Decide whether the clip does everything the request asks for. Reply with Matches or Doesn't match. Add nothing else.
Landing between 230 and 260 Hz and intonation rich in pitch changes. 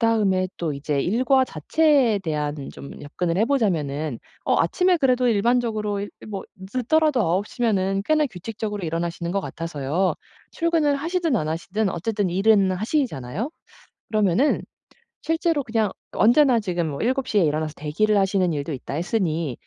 Doesn't match